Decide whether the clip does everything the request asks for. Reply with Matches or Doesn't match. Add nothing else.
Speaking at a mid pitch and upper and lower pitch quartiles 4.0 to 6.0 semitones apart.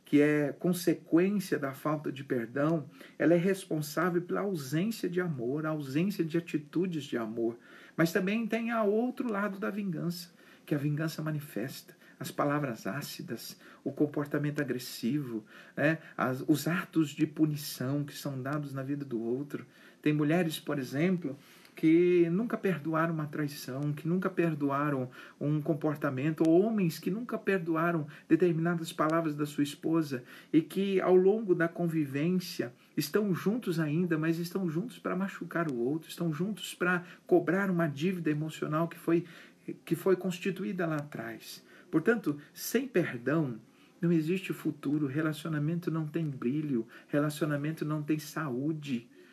Doesn't match